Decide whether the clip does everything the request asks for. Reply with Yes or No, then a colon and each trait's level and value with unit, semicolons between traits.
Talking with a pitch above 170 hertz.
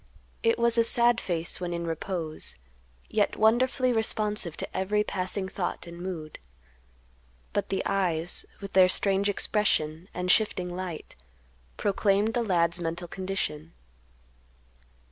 Yes: high, 190 Hz